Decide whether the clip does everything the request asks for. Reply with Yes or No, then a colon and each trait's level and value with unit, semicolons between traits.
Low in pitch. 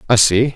Yes: low, 115 Hz